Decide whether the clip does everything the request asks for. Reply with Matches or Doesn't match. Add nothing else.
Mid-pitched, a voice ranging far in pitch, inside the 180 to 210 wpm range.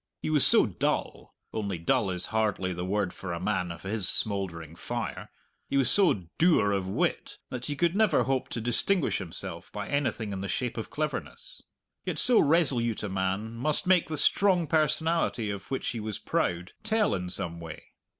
Doesn't match